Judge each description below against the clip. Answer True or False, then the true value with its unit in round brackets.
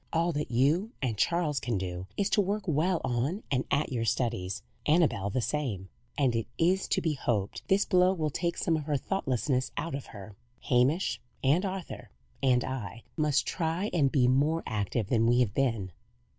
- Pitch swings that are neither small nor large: False (6.1 semitones)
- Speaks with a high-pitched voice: False (135 Hz)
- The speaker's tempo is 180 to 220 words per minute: True (185 wpm)